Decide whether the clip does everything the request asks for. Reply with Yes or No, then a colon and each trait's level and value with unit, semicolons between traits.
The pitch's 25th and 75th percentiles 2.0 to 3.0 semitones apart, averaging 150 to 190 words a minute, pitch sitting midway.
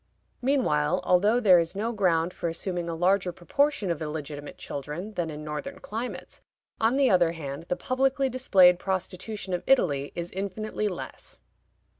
No: average, 4.8 semitones; average, 155 wpm; medium, 180 Hz